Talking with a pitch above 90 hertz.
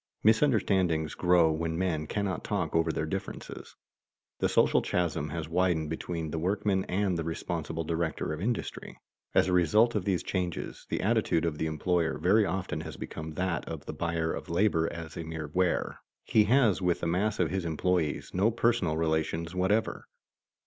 No: very low, 85 Hz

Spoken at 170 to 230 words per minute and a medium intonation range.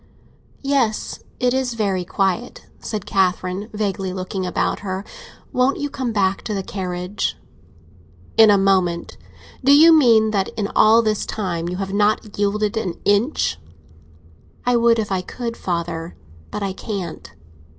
No: average, 145 wpm; average, 3.4 semitones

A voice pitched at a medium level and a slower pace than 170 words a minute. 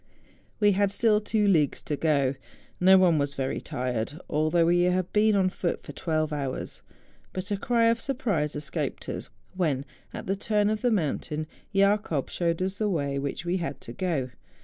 No: medium, 175 Hz; average, 190 wpm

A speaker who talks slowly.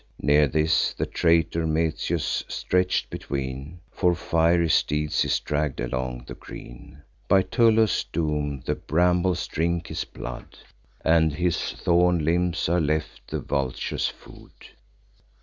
Yes: slow, 125 wpm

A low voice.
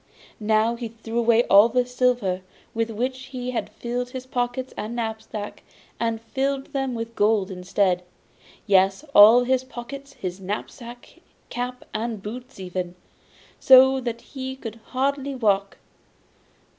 No: high, 235 Hz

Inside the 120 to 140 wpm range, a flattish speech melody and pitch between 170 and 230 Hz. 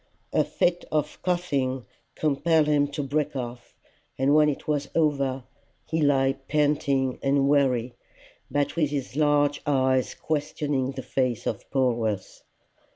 No: slow, 135 wpm; narrow, 2.2 semitones; medium, 140 Hz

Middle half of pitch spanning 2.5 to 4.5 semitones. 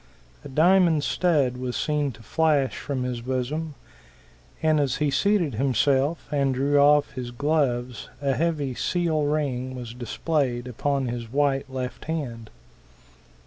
Yes: average, 3.2 semitones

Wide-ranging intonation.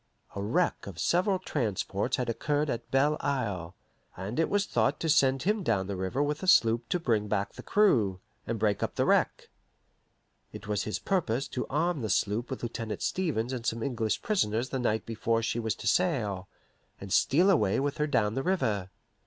Yes: wide, 6.0 semitones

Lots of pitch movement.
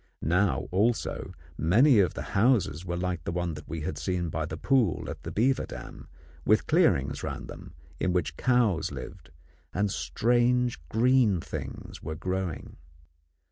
Yes: wide, 6.5 semitones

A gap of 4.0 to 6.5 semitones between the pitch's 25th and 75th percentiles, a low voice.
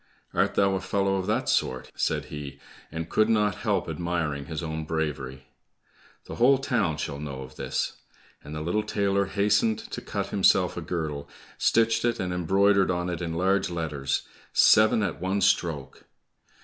Yes: average, 4.6 semitones; very low, 90 Hz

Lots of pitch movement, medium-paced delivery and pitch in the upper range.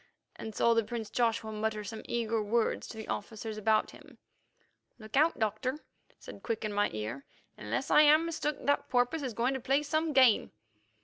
No: average, 3.8 semitones; average, 180 wpm; high, 230 Hz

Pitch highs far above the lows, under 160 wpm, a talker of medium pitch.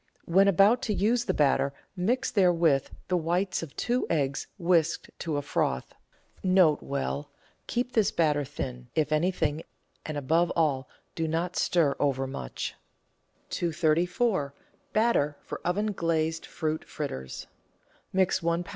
No: average, 4.3 semitones; slow, 135 wpm; medium, 165 Hz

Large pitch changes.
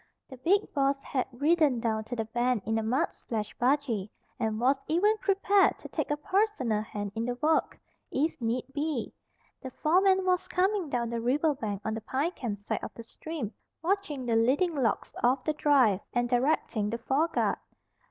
Yes: wide, 5.8 semitones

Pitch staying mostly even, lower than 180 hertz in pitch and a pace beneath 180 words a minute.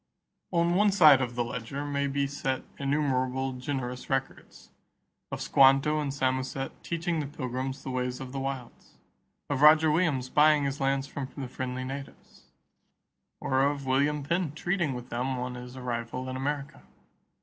Yes: narrow, 2.2 semitones; low, 135 Hz; average, 160 wpm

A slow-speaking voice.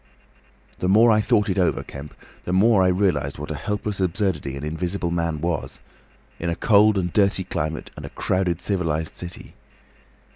No: average, 170 wpm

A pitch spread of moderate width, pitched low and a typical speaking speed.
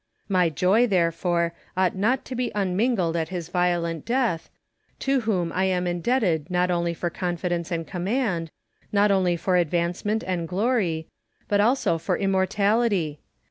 No: average, 3.3 semitones; medium, 180 Hz; average, 150 wpm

